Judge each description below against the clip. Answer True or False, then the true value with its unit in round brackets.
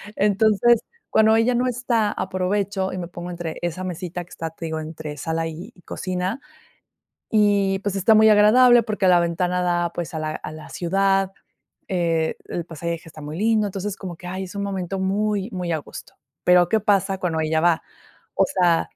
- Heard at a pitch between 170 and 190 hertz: True (185 Hz)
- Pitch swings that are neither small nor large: True (3.3 semitones)